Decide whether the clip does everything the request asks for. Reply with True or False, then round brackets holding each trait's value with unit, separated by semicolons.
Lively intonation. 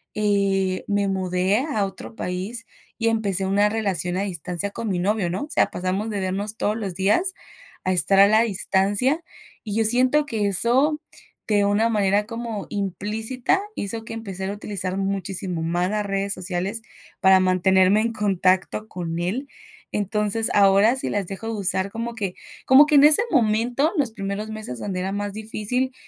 False (2.8 semitones)